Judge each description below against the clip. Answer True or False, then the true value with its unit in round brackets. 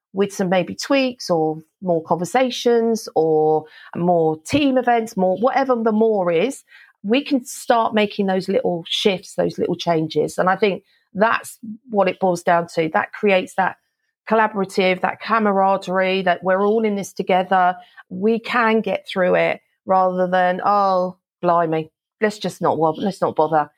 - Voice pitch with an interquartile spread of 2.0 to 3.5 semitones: False (3.9 semitones)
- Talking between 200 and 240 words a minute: False (160 wpm)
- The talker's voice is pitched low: False (190 Hz)